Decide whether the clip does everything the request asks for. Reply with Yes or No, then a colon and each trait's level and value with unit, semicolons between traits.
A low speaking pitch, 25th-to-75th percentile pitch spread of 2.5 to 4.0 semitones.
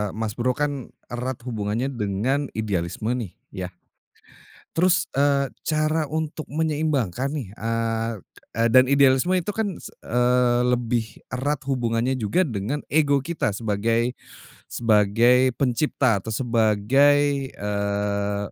No: low, 125 Hz; average, 4.5 semitones